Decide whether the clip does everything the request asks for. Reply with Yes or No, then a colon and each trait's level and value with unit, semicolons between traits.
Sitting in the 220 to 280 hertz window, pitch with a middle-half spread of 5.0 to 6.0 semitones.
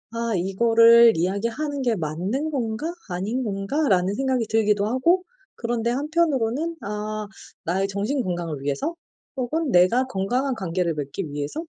Yes: high, 225 Hz; wide, 5.4 semitones